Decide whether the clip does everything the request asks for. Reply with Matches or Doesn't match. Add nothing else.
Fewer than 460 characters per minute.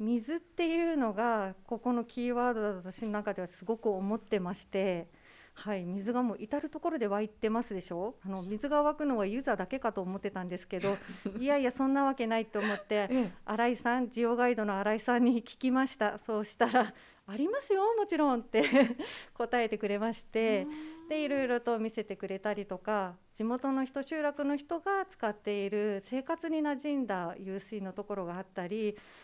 Matches